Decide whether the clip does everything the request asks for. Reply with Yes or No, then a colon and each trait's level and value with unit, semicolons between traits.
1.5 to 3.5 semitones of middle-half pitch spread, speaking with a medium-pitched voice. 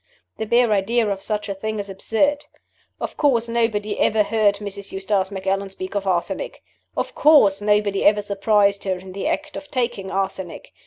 No: narrow, 2.4 semitones; high, 205 Hz